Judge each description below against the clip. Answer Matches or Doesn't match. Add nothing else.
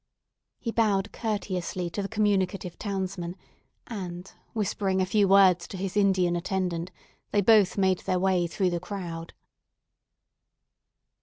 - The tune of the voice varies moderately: Doesn't match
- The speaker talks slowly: Matches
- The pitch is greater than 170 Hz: Matches